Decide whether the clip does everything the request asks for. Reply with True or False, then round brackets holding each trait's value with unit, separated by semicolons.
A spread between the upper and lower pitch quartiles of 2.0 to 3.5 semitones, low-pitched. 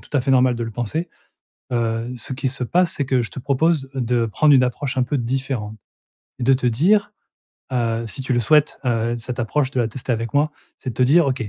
True (2.9 semitones; 125 Hz)